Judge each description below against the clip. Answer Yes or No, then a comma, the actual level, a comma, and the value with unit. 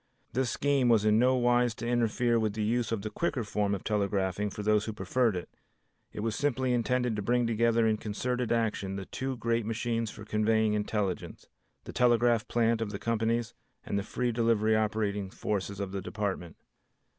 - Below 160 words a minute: No, average, 190 wpm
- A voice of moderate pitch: No, low, 110 Hz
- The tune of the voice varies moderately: No, narrow, 2.3 semitones